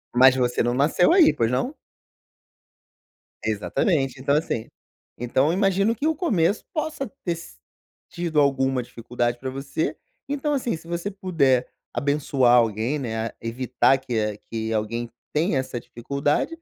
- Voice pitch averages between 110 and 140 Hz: Yes, low, 135 Hz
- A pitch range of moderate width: No, wide, 6.2 semitones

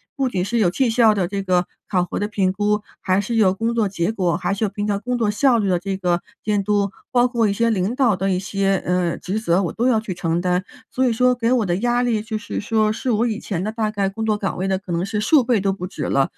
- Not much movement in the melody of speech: No, average, 3.4 semitones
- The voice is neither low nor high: No, high, 205 Hz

